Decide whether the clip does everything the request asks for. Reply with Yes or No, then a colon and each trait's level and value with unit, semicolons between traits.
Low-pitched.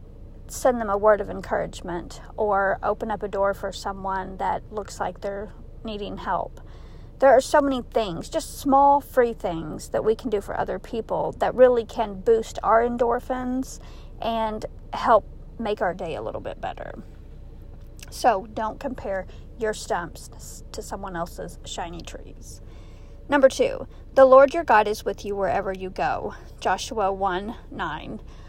No: high, 220 Hz